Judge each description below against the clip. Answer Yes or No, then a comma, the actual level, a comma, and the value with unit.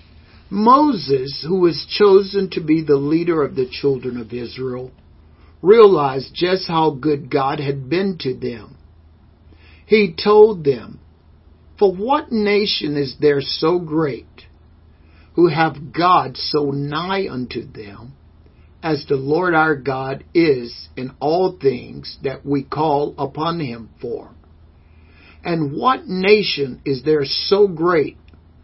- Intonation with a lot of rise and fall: Yes, wide, 8.1 semitones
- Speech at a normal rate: No, slow, 130 wpm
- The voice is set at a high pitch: No, medium, 140 Hz